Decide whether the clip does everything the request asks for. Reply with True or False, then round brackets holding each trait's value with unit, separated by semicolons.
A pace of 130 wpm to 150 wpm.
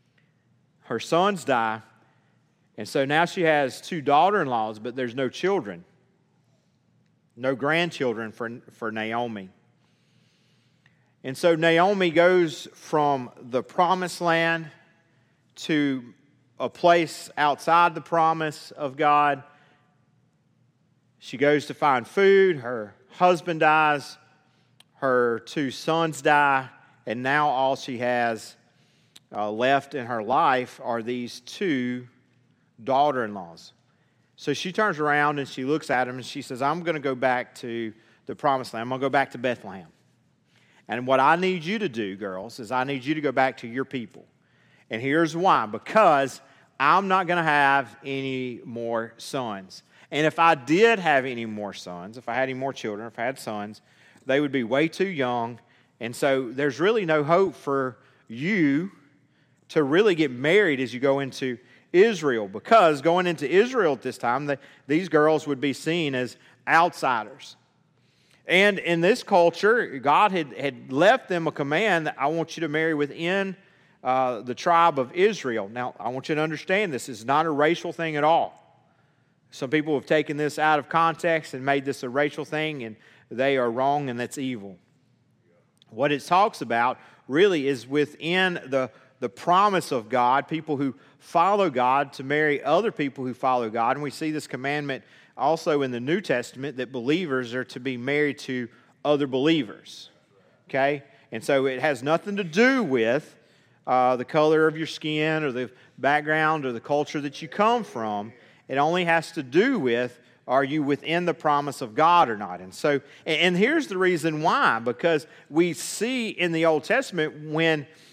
False (170 wpm)